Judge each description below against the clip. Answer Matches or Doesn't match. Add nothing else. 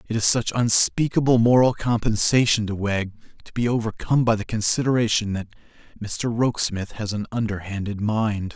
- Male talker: Matches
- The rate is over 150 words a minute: Doesn't match